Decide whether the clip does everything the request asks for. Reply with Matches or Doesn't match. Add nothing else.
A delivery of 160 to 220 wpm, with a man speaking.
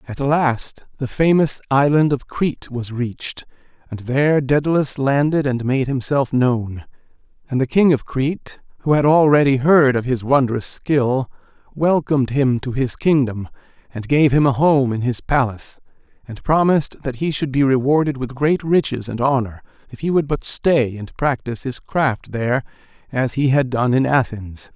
Matches